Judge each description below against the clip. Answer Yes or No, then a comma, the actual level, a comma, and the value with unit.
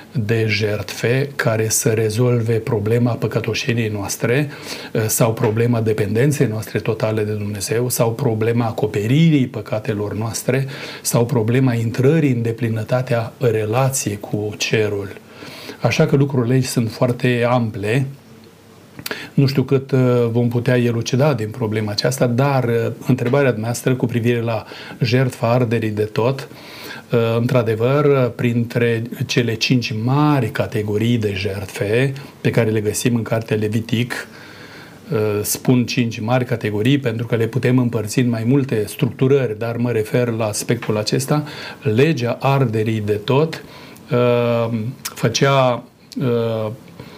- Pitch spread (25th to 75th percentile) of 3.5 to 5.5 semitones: No, average, 3.0 semitones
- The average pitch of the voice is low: Yes, low, 120 Hz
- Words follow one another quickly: No, average, 125 wpm